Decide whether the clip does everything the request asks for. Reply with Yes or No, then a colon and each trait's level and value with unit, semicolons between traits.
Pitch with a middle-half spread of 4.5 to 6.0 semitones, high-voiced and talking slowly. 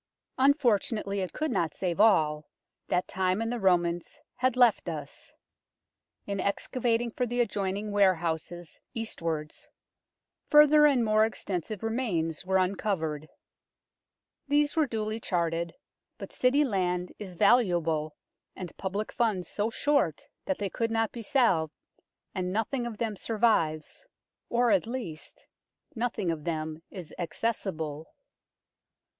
Yes: average, 5.3 semitones; high, 200 Hz; slow, 130 wpm